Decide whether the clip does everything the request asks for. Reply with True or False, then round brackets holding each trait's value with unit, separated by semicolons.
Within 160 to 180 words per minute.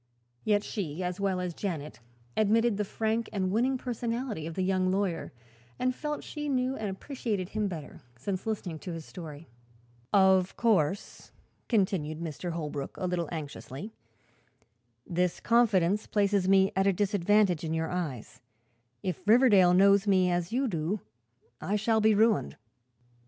False (145 wpm)